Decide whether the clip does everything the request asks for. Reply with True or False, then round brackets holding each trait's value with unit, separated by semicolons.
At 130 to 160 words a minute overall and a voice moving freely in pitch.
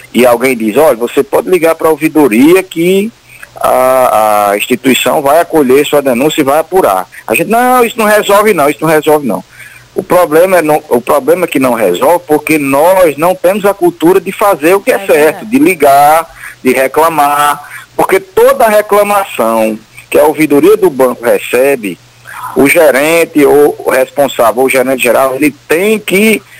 False (175 wpm; 6.5 semitones)